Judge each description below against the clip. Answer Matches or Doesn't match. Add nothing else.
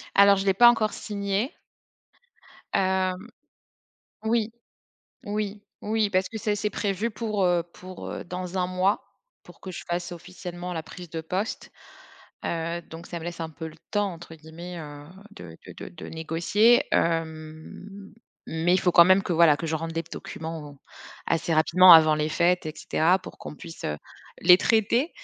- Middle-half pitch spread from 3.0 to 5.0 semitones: Matches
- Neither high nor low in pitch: Matches